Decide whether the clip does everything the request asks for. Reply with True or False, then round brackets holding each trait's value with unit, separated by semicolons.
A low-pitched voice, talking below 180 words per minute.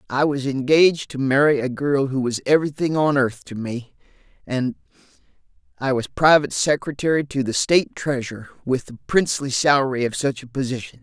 True (130 Hz; 165 wpm)